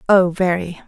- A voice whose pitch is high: No, medium, 180 Hz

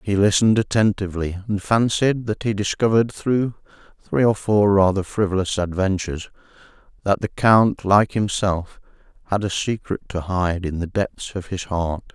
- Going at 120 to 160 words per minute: Yes, average, 155 wpm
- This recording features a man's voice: Yes, male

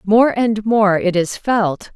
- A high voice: Yes, high, 210 Hz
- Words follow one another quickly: No, average, 185 wpm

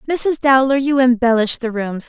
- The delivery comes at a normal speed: Yes, average, 175 wpm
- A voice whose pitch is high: Yes, very high, 255 Hz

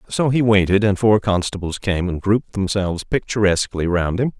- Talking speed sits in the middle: Yes, average, 180 wpm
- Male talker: Yes, male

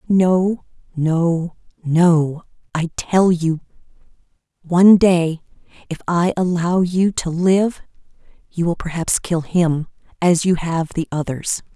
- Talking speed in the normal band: No, slow, 120 wpm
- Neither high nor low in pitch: Yes, medium, 170 Hz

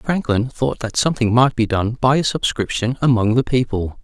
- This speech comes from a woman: No, male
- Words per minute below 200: Yes, average, 180 wpm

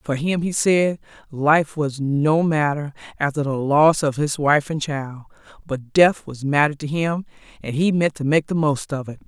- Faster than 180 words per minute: Yes, average, 200 wpm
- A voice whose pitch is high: No, medium, 150 Hz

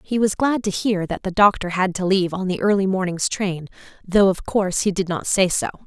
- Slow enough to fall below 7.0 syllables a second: Yes, 5.5 syllables/s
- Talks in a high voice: Yes, high, 195 Hz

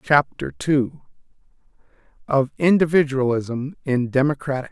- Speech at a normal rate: No, slow, 90 wpm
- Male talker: Yes, male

